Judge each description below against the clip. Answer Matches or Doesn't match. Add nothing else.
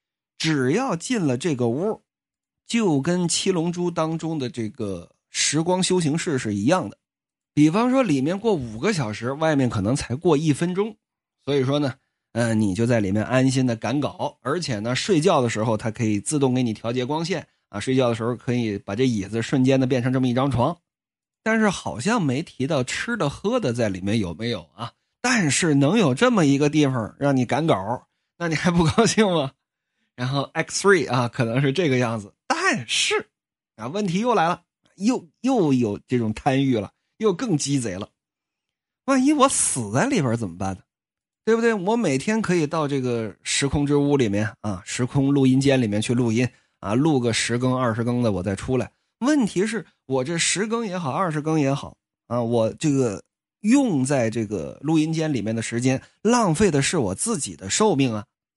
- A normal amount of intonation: Doesn't match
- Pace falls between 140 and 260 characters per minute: Doesn't match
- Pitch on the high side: Doesn't match